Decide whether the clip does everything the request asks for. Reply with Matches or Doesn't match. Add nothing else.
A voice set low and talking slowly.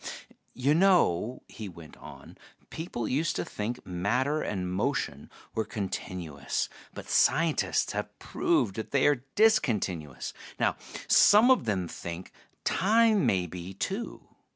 Matches